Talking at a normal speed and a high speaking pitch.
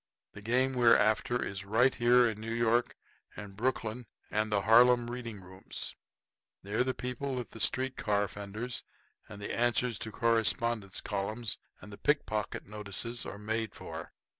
No: average, 160 wpm; low, 115 Hz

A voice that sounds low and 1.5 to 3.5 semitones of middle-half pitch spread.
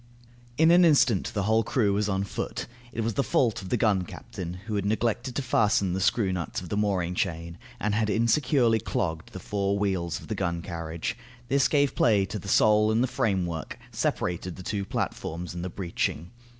No: low, 100 Hz; average, 3.9 semitones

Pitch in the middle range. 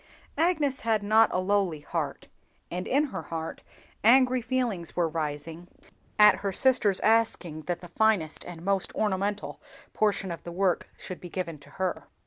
No: high, 195 Hz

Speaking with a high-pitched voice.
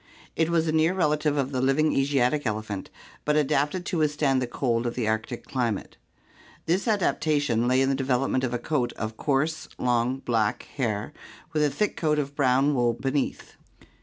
No: low, 135 Hz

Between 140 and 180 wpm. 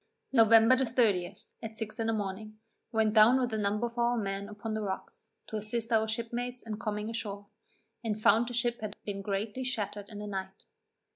No: average, 200 wpm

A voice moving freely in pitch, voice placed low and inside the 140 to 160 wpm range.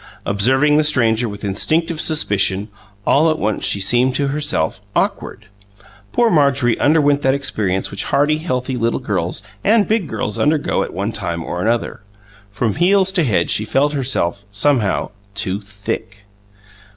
Yes: wide, 6.4 semitones; low, 125 Hz; average, 150 wpm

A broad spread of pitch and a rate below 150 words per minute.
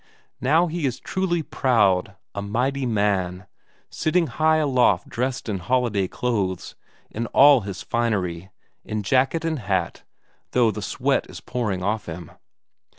Yes: wide, 5.7 semitones; average, 140 wpm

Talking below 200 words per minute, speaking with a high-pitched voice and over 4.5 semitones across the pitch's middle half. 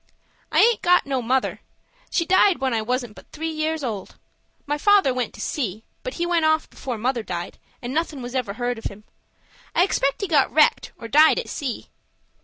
No: fast, 205 wpm; very high, 270 Hz; average, 4.9 semitones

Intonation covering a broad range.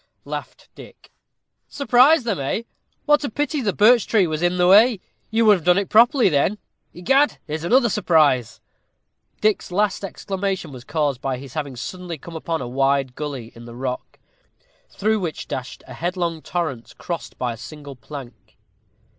Yes: wide, 7.4 semitones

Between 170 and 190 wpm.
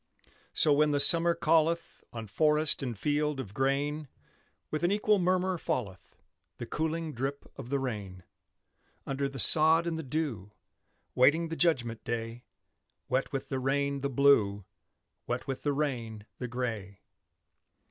No: average, 145 wpm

